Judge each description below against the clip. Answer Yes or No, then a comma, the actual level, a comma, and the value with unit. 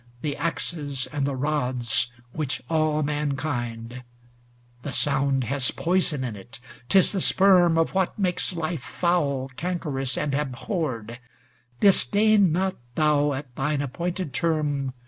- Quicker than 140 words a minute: No, slow, 135 wpm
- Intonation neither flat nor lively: Yes, average, 4.3 semitones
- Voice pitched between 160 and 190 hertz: No, medium, 145 Hz